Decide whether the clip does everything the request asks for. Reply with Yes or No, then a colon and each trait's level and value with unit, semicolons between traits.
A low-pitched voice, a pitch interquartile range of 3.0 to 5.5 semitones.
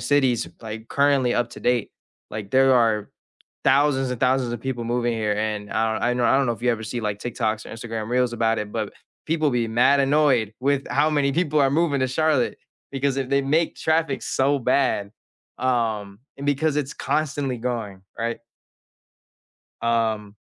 Yes: low, 125 Hz; average, 3.7 semitones